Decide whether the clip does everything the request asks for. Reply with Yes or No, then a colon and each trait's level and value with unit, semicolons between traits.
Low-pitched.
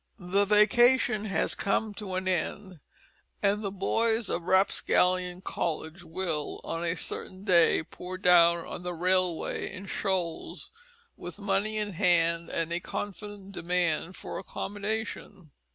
No: medium, 185 Hz